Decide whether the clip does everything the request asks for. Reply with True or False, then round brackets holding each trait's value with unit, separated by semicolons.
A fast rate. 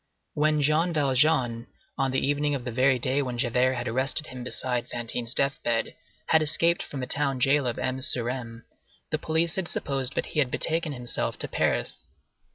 False (190 wpm)